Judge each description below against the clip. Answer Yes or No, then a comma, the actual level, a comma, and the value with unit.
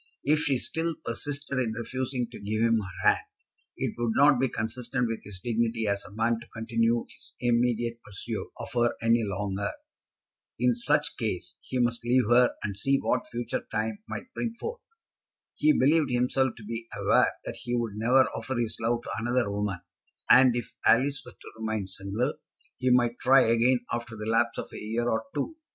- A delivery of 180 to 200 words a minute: Yes, average, 190 wpm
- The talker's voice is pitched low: Yes, low, 120 Hz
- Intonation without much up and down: Yes, narrow, 2.3 semitones